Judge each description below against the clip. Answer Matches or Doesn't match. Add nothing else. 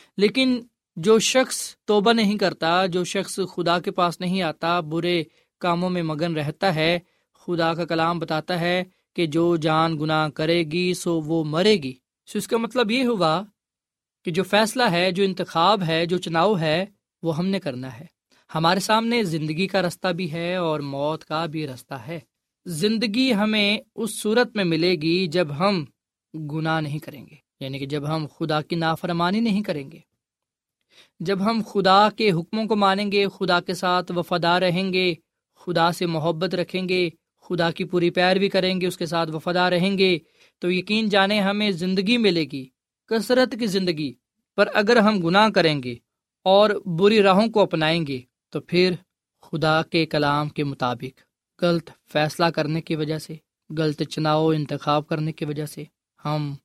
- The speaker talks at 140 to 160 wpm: Doesn't match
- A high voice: Doesn't match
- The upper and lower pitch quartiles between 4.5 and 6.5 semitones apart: Doesn't match